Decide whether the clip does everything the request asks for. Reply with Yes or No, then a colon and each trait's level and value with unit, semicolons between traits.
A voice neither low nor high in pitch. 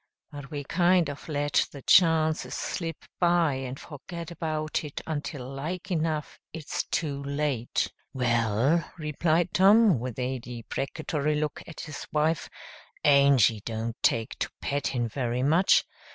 Yes: medium, 145 Hz